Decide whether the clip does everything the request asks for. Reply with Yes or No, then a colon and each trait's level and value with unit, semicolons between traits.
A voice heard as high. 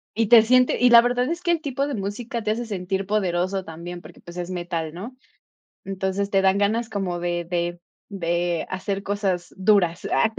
Yes: high, 195 Hz